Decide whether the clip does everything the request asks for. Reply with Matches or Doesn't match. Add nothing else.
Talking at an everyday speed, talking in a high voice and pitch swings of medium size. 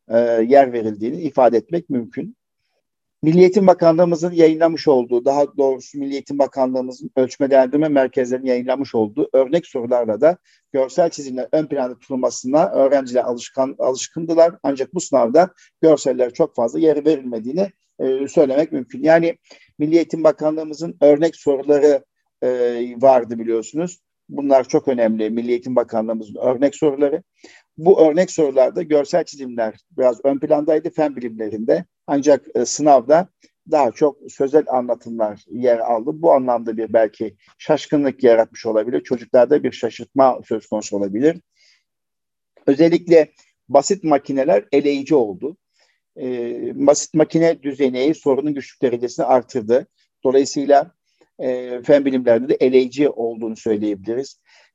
Doesn't match